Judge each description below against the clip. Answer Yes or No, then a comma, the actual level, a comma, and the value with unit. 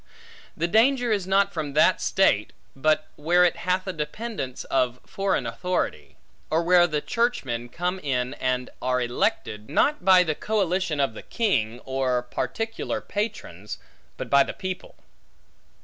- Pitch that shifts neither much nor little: No, wide, 7.0 semitones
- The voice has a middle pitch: Yes, medium, 160 Hz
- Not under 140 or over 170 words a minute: Yes, average, 150 wpm